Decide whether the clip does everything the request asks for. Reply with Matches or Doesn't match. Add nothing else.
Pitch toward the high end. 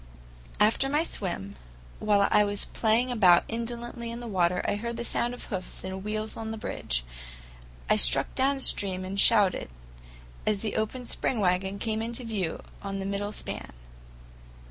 Matches